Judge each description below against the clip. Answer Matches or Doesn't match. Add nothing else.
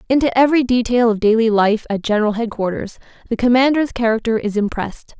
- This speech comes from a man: Doesn't match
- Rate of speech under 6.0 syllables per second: Doesn't match